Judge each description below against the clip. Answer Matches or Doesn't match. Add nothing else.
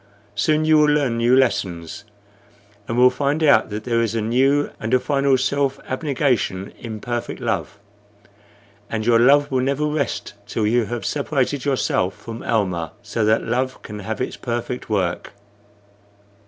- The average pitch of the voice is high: Doesn't match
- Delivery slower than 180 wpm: Matches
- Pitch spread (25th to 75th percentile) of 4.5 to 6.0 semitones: Doesn't match